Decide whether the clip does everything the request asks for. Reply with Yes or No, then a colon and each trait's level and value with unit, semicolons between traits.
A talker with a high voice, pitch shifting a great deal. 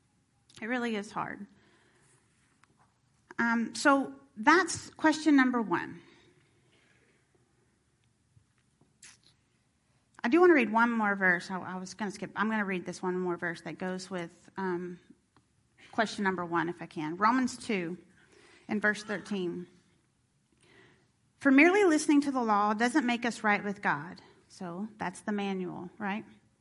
No: high, 205 Hz; average, 4.9 semitones